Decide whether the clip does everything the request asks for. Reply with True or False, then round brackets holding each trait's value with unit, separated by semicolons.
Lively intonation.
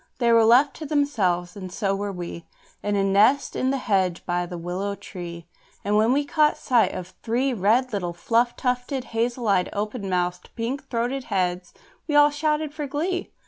True (6.2 semitones)